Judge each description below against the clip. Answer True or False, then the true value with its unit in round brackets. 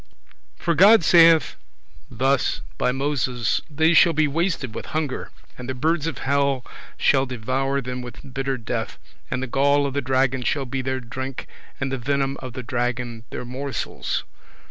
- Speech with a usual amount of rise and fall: False (2.2 semitones)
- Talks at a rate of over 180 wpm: False (165 wpm)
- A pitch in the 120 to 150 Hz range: True (135 Hz)